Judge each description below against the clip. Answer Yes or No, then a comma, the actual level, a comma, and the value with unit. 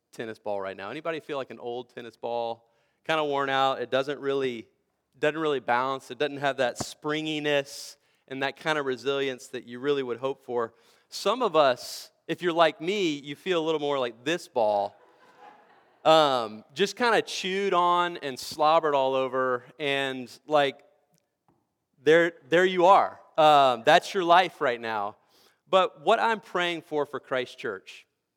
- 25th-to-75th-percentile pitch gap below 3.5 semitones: No, average, 4.3 semitones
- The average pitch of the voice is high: No, medium, 140 Hz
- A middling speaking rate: Yes, average, 175 wpm